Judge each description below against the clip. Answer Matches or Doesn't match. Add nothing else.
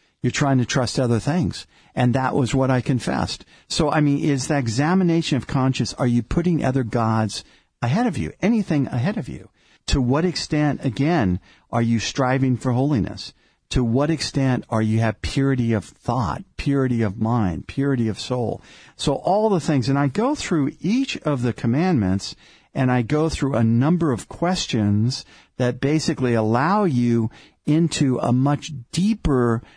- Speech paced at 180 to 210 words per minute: Doesn't match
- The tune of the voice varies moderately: Matches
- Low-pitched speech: Matches